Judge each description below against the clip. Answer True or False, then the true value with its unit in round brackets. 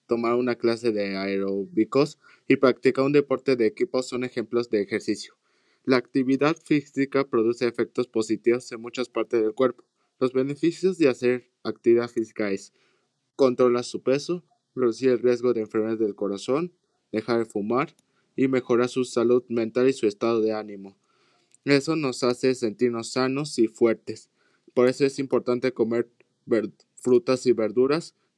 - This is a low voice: True (125 Hz)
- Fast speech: False (150 wpm)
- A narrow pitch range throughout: True (2.2 semitones)